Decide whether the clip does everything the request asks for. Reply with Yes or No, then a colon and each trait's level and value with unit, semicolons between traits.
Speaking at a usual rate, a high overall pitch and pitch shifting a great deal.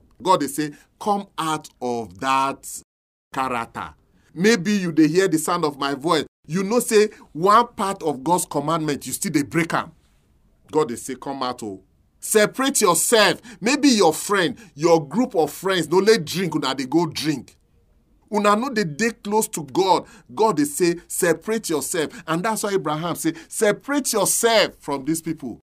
No: average, 175 wpm; medium, 170 Hz; wide, 6.9 semitones